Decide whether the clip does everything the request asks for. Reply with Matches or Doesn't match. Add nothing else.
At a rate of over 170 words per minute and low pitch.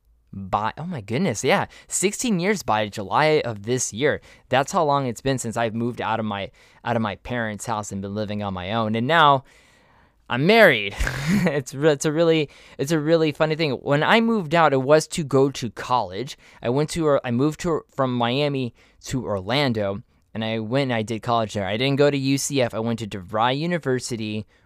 Matches